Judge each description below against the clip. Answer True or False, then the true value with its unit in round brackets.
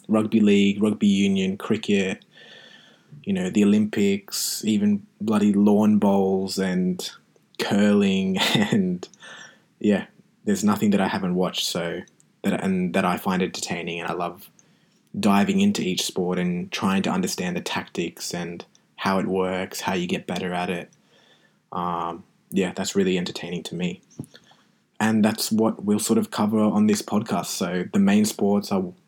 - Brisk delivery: False (150 wpm)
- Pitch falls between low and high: False (110 Hz)